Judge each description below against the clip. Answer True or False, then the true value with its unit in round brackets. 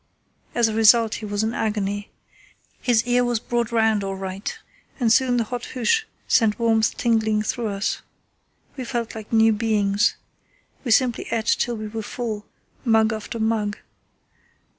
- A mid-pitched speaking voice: False (225 Hz)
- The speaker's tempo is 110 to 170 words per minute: True (160 wpm)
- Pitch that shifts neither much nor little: False (1.9 semitones)